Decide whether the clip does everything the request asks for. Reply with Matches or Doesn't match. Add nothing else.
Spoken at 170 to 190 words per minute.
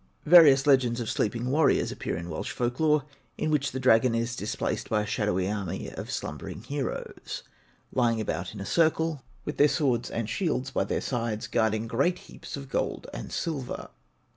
Matches